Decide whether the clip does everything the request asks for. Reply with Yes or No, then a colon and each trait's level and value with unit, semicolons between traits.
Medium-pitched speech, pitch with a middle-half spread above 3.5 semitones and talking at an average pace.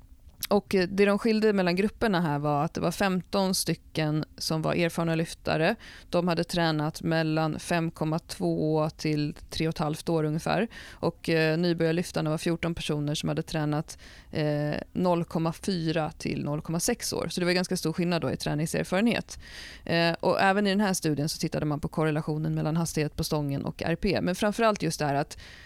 No: medium, 165 Hz; narrow, 2.4 semitones; average, 160 wpm